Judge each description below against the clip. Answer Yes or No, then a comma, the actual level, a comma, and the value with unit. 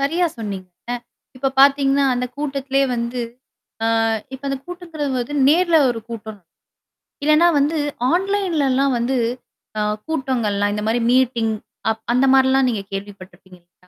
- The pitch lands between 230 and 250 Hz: No, very high, 265 Hz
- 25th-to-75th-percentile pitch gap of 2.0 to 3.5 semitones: No, average, 4.3 semitones